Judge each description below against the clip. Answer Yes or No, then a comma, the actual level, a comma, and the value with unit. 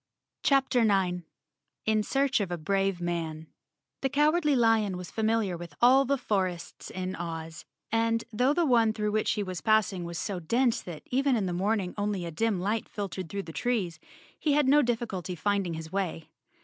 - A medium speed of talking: Yes, average, 190 wpm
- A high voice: Yes, high, 205 Hz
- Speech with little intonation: No, average, 5.0 semitones